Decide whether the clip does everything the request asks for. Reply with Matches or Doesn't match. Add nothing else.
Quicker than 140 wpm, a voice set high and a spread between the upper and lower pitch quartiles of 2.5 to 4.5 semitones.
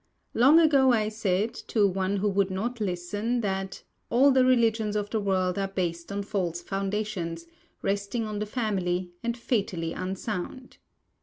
Matches